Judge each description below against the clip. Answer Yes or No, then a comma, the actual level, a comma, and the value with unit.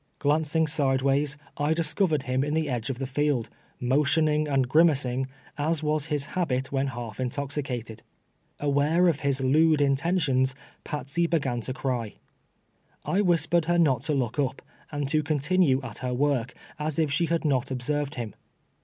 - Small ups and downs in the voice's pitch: No, average, 3.0 semitones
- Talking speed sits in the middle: Yes, average, 160 wpm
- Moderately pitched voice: Yes, medium, 145 Hz